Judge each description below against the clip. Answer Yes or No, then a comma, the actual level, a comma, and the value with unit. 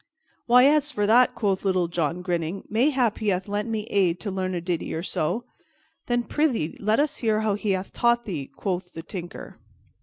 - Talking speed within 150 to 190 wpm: No, average, 200 wpm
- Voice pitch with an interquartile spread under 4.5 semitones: No, average, 4.8 semitones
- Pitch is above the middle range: Yes, high, 200 Hz